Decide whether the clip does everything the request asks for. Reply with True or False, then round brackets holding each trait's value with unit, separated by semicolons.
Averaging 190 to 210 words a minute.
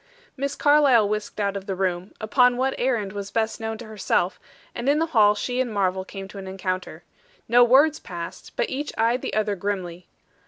True (200 wpm)